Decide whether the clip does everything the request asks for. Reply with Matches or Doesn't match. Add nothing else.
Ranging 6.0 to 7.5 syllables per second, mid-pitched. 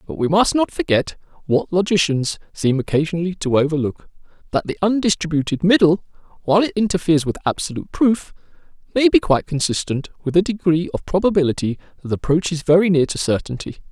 Matches